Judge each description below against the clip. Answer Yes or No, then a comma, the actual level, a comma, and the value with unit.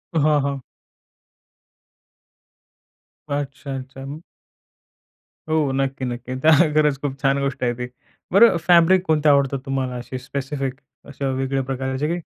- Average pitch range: No, narrow, 2.1 semitones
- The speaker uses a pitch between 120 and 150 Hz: Yes, low, 135 Hz